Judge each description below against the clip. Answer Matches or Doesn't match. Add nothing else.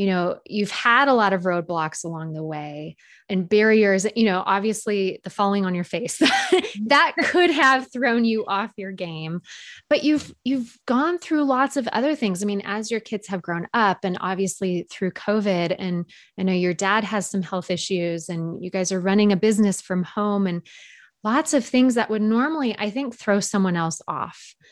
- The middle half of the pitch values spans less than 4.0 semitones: Doesn't match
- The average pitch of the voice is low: Doesn't match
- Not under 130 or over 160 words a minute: Doesn't match